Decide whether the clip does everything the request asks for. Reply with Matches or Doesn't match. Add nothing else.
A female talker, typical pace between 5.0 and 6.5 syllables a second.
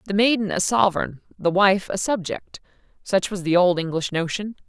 Matches